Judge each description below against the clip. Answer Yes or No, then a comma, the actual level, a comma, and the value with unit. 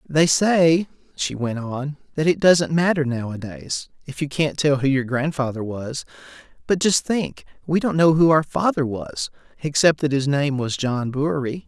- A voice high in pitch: No, medium, 145 Hz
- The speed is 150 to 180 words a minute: Yes, average, 170 wpm